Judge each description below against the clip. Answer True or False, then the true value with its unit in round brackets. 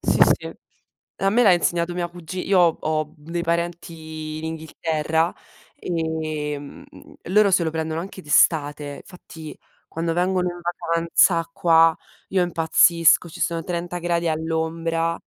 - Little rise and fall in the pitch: True (1.6 semitones)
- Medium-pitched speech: True (165 Hz)